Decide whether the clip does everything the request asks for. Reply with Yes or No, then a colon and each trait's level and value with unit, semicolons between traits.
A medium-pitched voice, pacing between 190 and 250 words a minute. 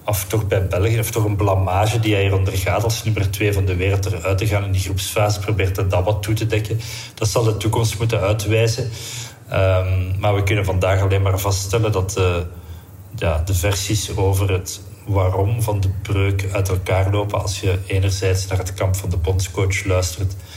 No: low, 100 Hz; fast, 200 wpm